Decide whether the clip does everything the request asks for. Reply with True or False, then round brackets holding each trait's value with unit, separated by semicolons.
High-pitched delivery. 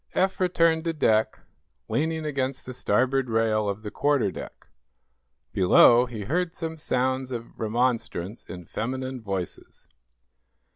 False (125 Hz)